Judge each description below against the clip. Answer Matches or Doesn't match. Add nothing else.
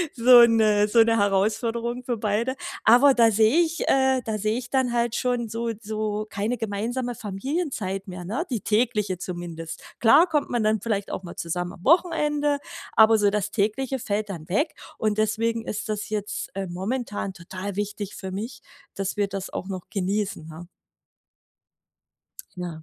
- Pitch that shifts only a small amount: Doesn't match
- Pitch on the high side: Matches